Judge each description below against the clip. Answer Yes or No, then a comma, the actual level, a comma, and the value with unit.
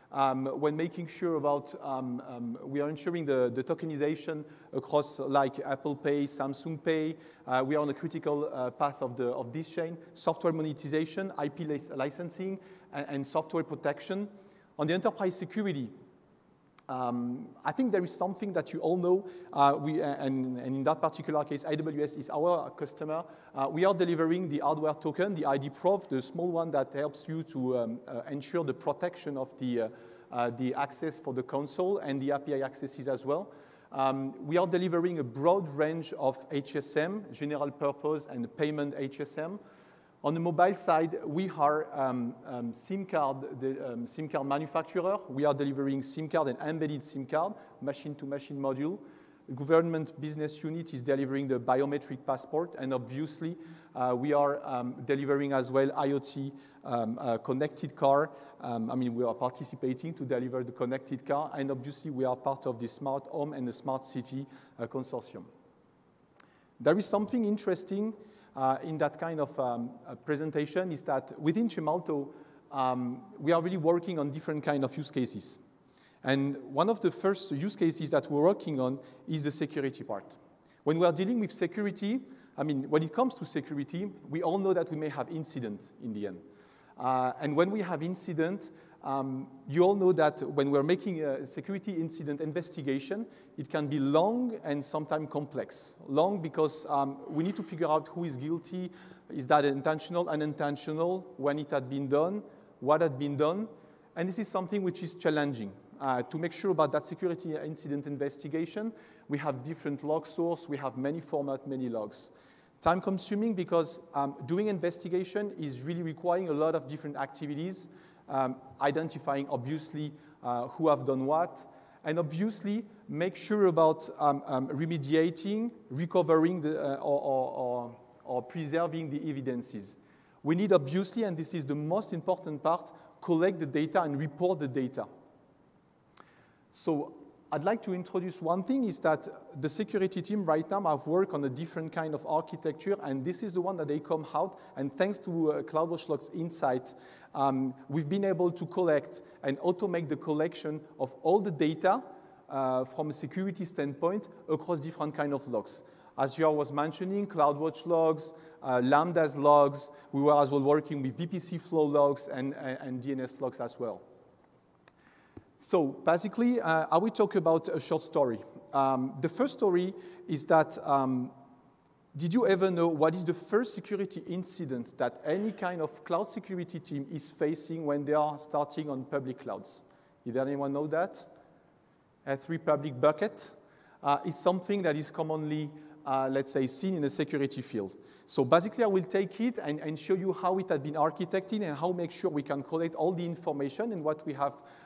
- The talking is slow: No, average, 175 wpm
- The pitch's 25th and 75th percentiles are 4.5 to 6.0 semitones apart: No, average, 3.8 semitones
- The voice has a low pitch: No, medium, 155 Hz